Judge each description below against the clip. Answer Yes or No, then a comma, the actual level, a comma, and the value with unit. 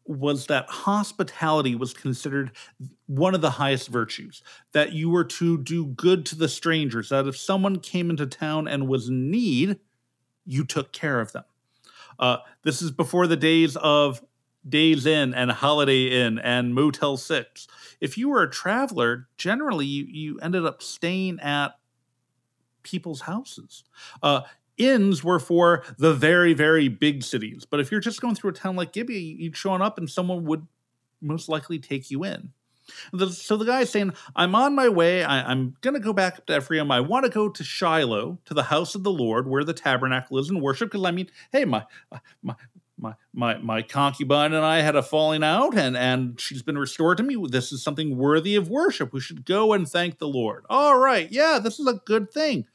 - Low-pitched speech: No, medium, 155 Hz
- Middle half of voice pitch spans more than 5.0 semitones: Yes, wide, 5.4 semitones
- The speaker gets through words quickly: No, average, 195 wpm